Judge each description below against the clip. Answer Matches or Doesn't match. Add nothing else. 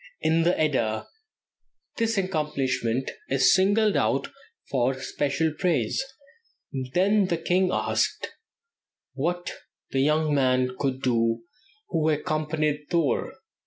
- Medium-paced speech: Doesn't match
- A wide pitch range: Doesn't match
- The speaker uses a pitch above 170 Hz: Doesn't match